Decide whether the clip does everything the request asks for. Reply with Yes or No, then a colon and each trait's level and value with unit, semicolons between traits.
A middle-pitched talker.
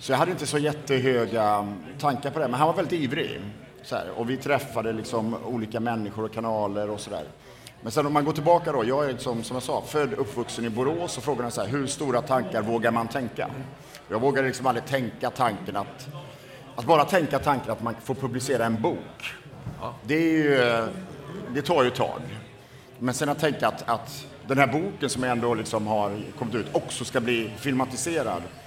No: low, 130 Hz